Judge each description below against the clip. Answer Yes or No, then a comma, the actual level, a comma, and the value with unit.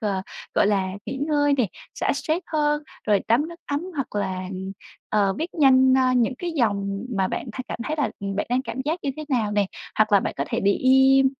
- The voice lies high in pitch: Yes, very high, 255 Hz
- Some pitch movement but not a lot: No, wide, 6.2 semitones